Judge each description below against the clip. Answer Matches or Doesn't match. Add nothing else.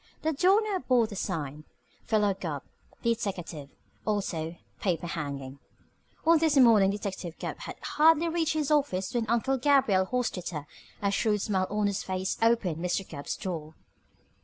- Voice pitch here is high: Matches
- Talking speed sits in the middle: Matches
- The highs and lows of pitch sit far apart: Matches